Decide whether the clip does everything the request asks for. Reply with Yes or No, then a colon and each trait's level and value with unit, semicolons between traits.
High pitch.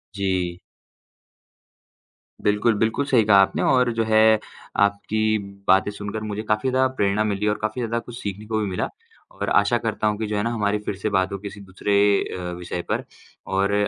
No: low, 105 Hz